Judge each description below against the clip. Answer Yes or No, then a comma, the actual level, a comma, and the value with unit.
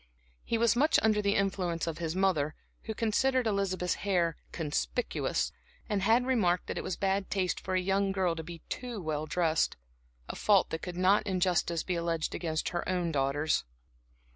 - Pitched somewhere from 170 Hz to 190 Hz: Yes, medium, 185 Hz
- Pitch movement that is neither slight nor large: Yes, average, 3.3 semitones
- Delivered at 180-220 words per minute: Yes, average, 185 wpm